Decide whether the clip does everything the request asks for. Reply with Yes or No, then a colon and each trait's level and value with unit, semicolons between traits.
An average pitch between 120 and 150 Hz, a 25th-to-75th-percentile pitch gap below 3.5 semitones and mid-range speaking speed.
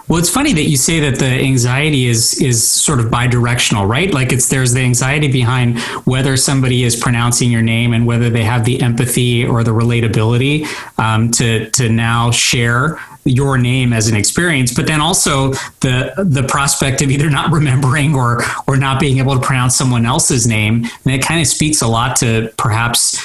Yes: low, 130 Hz; average, 3.0 semitones; average, 195 wpm